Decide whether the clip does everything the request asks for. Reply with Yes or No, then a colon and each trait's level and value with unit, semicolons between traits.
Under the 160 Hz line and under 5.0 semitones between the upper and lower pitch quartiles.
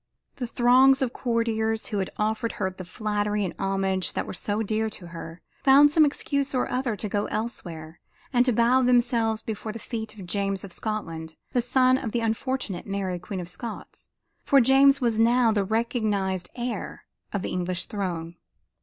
No: high, 220 Hz; average, 4.1 semitones